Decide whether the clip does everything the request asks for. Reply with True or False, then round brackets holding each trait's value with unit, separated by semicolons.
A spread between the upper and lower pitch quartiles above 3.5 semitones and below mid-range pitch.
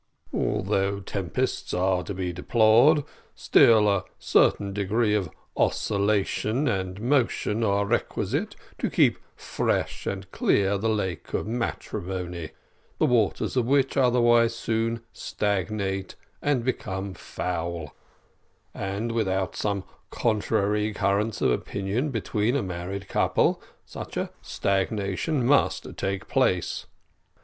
False (3.2 semitones; 100 Hz)